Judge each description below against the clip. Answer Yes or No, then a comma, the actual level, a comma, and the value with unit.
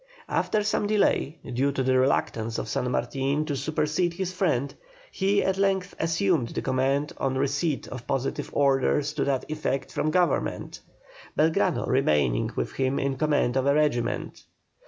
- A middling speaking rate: Yes, average, 155 wpm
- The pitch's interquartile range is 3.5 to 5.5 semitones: Yes, average, 4.0 semitones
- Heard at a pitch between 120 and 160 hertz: Yes, medium, 140 Hz